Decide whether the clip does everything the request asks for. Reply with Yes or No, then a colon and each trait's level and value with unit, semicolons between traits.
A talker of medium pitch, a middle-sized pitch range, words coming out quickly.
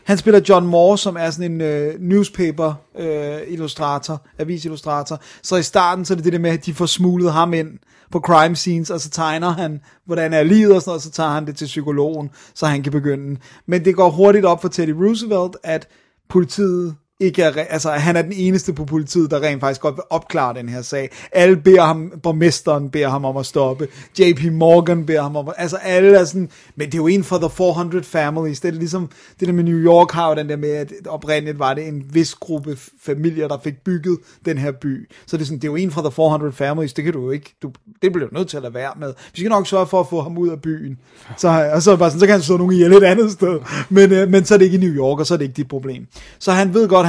Yes: medium, 165 Hz; average, 3.3 semitones; fast, 265 wpm